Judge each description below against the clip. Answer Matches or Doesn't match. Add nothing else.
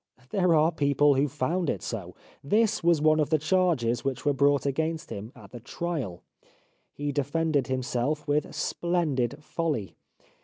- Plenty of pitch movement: Doesn't match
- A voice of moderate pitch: Matches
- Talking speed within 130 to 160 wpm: Matches